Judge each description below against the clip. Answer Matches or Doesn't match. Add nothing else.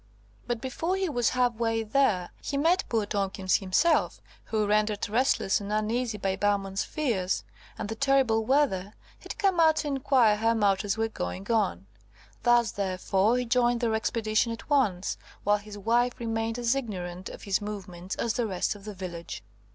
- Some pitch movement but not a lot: Matches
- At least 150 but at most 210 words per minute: Matches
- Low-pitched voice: Doesn't match